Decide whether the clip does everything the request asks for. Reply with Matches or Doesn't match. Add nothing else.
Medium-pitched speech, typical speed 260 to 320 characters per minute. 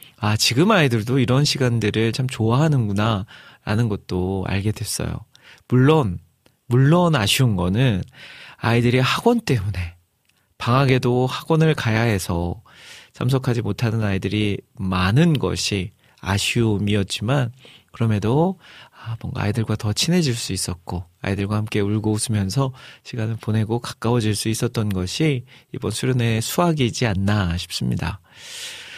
Doesn't match